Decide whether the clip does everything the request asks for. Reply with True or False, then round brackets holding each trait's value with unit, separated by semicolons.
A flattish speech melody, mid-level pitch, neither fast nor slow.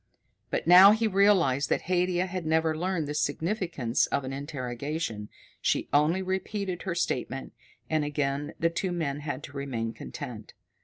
False (4.6 semitones; 160 Hz; 155 wpm)